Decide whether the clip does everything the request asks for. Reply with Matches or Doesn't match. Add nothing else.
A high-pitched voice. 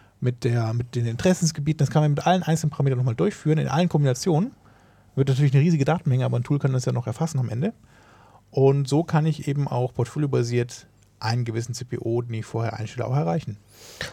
Doesn't match